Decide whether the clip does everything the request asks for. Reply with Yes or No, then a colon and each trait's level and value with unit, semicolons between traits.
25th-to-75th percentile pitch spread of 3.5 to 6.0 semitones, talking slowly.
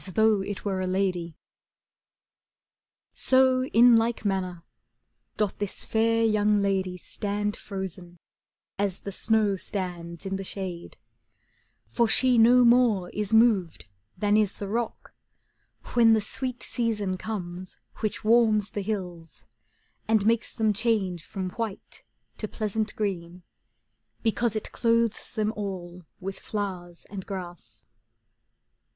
No: average, 3.1 semitones; slow, 120 wpm